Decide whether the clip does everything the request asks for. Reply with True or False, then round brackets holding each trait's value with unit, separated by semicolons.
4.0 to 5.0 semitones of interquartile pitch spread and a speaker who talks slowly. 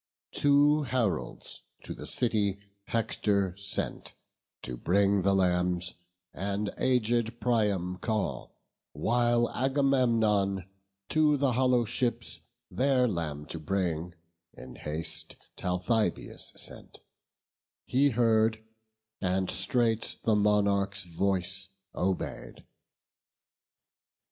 True (4.4 semitones; 90 wpm)